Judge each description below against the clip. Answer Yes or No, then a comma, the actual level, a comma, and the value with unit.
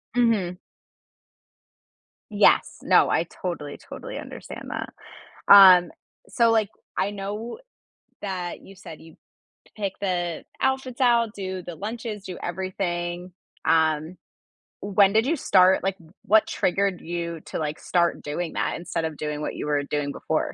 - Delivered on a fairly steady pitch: No, average, 3.4 semitones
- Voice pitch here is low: No, medium, 185 Hz